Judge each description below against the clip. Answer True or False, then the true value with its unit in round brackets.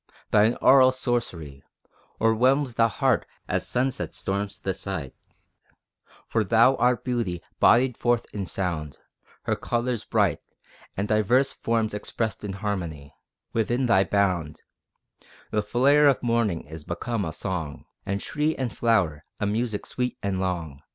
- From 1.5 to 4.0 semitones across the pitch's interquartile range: False (4.6 semitones)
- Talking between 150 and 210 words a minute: False (140 wpm)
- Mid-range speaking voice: False (105 Hz)